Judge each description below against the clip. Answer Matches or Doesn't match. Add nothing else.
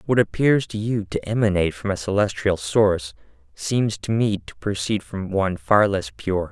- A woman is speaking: Doesn't match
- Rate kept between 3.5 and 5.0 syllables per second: Matches